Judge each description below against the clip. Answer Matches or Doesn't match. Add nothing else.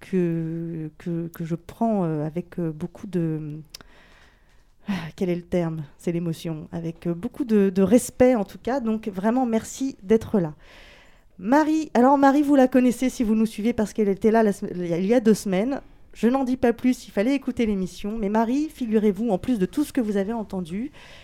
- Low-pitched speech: Doesn't match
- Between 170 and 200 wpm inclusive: Matches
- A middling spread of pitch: Doesn't match